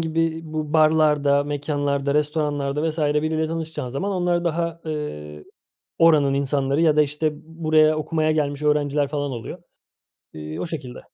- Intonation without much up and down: Yes, narrow, 2.0 semitones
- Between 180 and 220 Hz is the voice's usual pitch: No, medium, 150 Hz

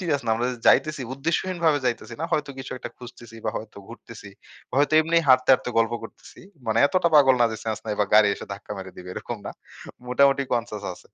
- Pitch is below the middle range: Yes, low, 125 Hz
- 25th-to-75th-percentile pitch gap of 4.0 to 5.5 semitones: Yes, average, 4.6 semitones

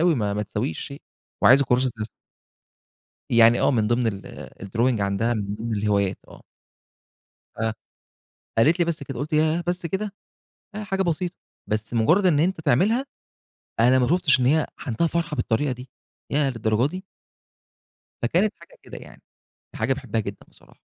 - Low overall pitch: Yes, low, 130 Hz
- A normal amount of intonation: No, wide, 6.9 semitones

